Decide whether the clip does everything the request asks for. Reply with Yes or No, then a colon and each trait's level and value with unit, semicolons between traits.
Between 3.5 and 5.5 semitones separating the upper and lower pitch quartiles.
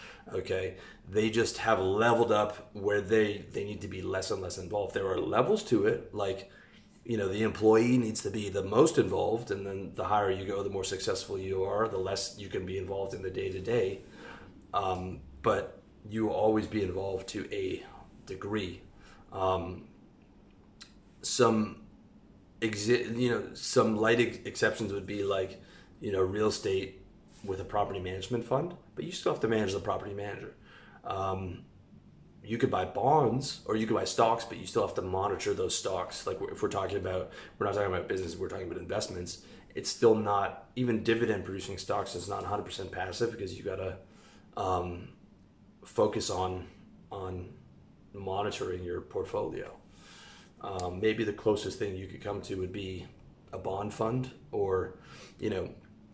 No: average, 3.0 semitones